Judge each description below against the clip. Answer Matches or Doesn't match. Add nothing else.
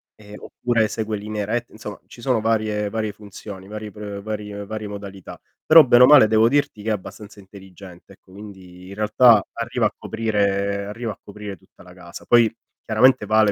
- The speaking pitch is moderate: Doesn't match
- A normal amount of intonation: Doesn't match